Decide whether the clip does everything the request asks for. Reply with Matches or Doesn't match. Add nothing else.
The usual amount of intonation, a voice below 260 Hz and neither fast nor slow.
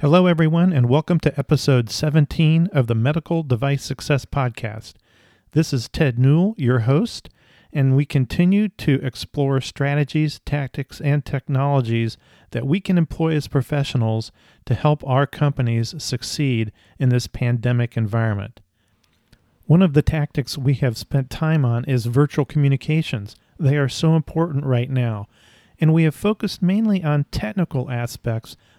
Matches